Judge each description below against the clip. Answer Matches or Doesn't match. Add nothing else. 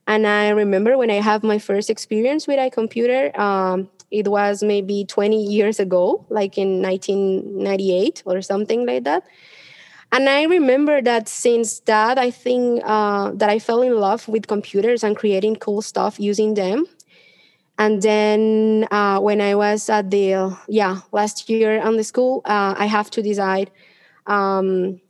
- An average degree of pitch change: Doesn't match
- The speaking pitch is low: Doesn't match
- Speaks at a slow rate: Doesn't match